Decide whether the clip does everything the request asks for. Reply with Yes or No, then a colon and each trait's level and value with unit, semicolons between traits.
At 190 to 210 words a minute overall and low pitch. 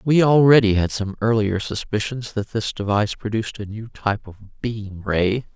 No: average, 175 wpm; low, 110 Hz